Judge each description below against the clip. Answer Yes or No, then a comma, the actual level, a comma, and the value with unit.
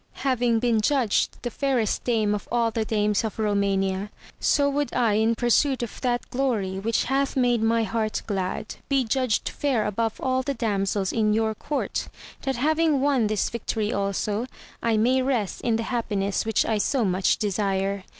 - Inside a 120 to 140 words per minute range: No, average, 175 wpm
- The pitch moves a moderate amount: Yes, average, 3.4 semitones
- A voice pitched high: Yes, high, 225 Hz